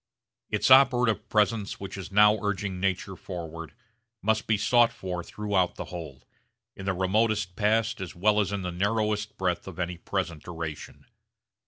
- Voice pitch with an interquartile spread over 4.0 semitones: No, average, 3.0 semitones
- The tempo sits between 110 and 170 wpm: Yes, average, 160 wpm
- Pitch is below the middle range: Yes, low, 100 Hz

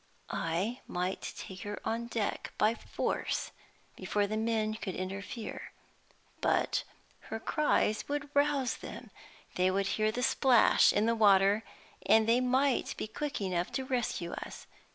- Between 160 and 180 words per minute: No, average, 145 wpm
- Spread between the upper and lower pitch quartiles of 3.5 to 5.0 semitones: Yes, average, 3.9 semitones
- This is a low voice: No, high, 220 Hz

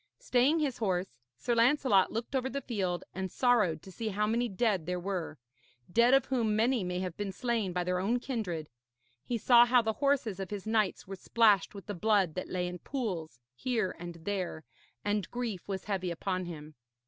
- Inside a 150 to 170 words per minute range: No, average, 195 wpm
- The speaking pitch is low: No, high, 205 Hz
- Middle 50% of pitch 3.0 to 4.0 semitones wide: No, average, 4.6 semitones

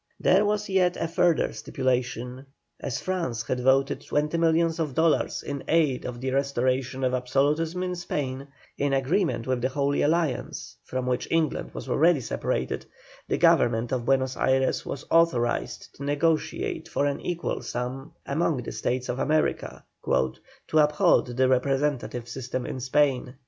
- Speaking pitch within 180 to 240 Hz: No, low, 135 Hz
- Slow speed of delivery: No, average, 155 wpm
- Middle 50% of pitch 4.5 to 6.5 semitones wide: No, average, 4.0 semitones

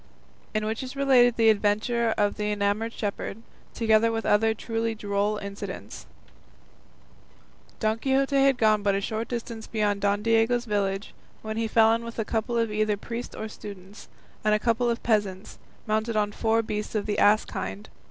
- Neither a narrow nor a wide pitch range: No, narrow, 1.7 semitones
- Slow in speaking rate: No, average, 175 wpm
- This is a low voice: No, high, 220 Hz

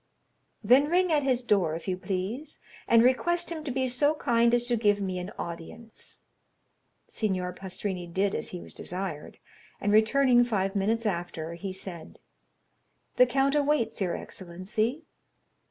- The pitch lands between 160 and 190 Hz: No, high, 215 Hz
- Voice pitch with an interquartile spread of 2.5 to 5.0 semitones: No, wide, 5.4 semitones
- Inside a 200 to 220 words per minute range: No, average, 155 wpm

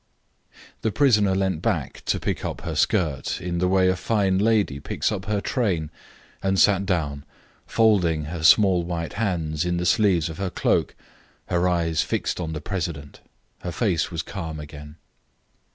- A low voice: Yes, very low, 90 Hz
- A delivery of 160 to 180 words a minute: Yes, average, 170 wpm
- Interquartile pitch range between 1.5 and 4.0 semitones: Yes, average, 3.4 semitones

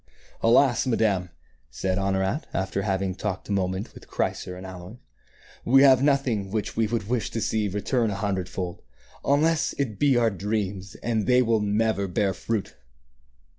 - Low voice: Yes, low, 105 Hz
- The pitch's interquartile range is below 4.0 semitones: Yes, average, 3.6 semitones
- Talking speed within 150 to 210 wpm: Yes, average, 170 wpm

